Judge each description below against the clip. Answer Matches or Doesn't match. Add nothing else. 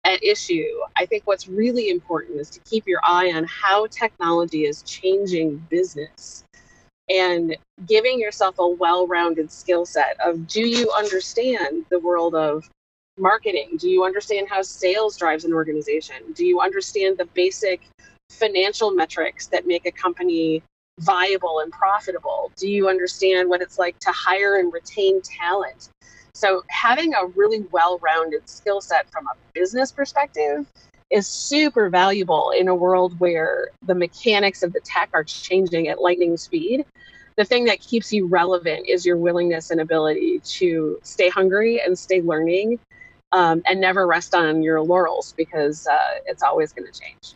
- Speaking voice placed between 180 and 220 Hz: Matches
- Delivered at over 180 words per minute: Doesn't match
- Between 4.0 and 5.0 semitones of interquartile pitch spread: Matches